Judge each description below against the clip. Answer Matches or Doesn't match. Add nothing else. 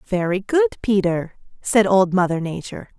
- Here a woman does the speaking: Matches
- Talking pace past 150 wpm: Doesn't match